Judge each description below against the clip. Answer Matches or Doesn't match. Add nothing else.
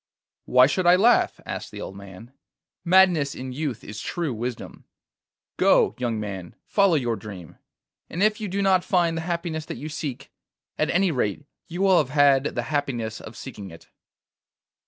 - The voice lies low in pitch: Doesn't match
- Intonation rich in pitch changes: Matches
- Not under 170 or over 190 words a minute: Matches